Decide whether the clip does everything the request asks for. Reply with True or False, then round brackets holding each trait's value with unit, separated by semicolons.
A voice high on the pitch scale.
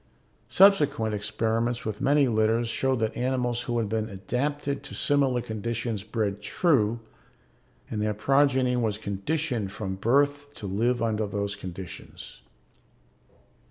False (115 Hz)